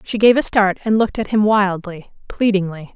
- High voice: Yes, high, 200 Hz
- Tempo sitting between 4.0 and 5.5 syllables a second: Yes, 5.3 syllables/s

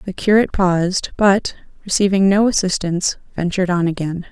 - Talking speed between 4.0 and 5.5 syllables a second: No, 5.7 syllables/s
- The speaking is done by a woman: Yes, female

